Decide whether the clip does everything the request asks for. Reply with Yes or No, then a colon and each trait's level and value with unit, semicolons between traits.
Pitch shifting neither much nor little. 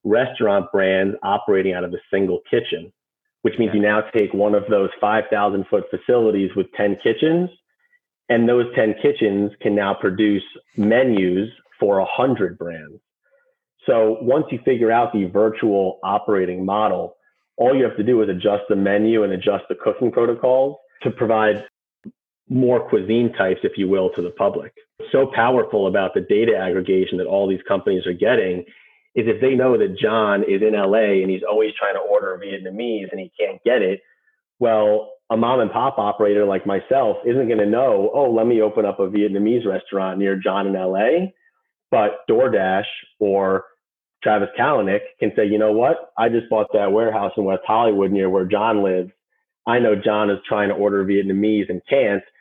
No: wide, 8.2 semitones